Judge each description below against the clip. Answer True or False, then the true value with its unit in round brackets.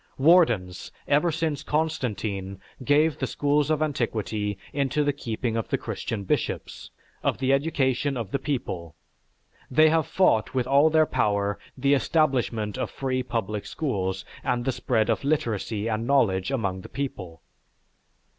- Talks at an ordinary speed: True (145 wpm)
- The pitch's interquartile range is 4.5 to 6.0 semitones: True (5.4 semitones)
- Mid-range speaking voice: False (130 Hz)